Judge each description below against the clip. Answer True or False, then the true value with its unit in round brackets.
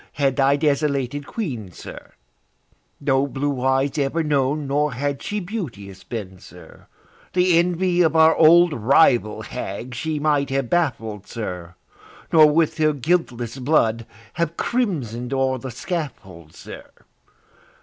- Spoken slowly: True (130 wpm)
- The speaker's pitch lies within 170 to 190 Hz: False (140 Hz)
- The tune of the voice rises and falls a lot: False (4.7 semitones)